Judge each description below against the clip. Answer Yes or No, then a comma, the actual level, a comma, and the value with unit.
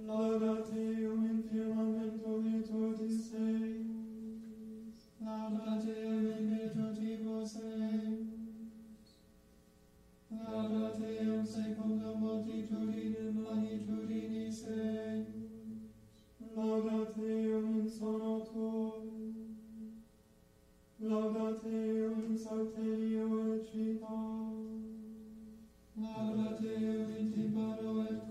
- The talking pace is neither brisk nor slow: No, slow, 75 wpm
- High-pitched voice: Yes, high, 220 Hz